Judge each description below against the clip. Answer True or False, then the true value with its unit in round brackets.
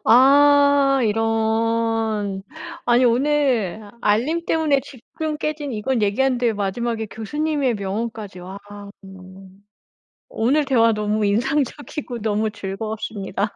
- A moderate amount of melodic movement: True (4.4 semitones)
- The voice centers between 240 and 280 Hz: False (230 Hz)